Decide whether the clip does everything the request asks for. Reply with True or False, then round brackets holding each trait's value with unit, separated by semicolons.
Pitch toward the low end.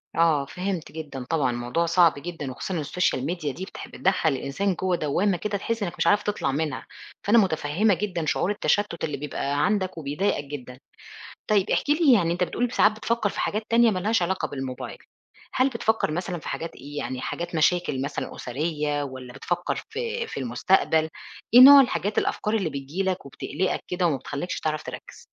False (170 Hz)